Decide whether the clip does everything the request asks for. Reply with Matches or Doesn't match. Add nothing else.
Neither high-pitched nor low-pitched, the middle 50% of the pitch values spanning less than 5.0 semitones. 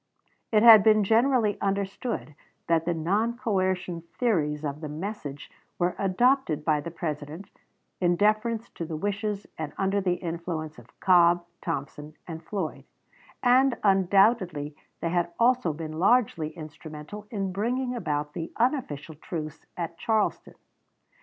Doesn't match